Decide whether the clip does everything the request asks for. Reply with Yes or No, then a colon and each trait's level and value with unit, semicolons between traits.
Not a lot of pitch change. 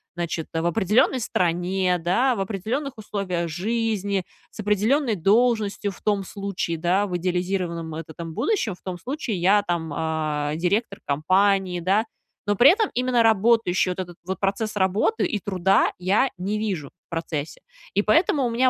No: average, 3.9 semitones